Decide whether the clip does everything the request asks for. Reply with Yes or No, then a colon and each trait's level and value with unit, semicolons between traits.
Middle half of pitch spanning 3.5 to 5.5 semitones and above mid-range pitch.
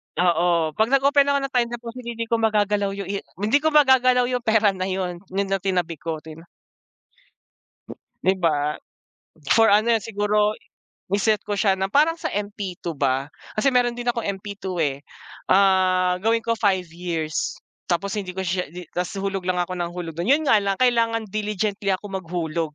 Yes: average, 4.1 semitones; high, 200 Hz